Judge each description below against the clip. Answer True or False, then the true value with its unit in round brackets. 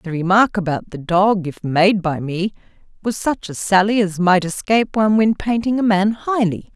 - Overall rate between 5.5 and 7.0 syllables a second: False (4.9 syllables/s)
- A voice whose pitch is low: False (195 Hz)